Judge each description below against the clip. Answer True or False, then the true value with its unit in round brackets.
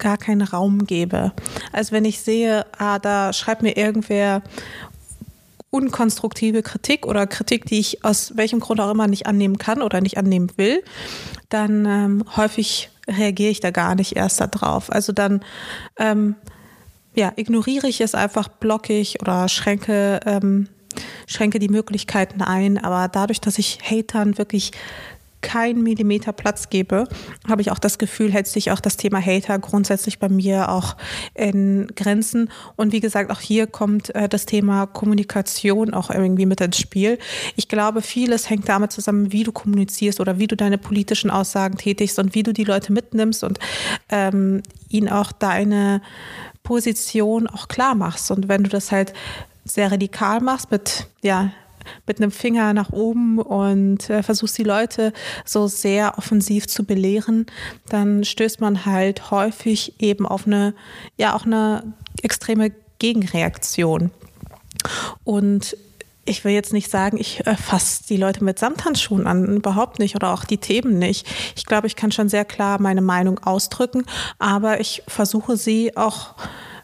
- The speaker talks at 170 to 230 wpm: False (160 wpm)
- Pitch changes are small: True (1.7 semitones)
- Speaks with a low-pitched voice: False (210 Hz)